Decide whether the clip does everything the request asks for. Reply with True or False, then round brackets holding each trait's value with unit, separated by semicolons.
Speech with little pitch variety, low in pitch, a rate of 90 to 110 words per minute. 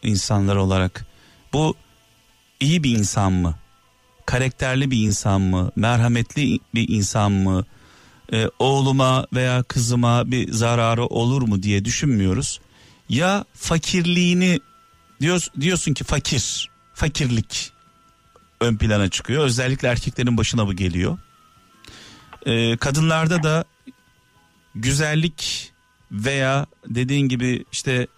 False (4.7 semitones; 120 Hz; 100 wpm)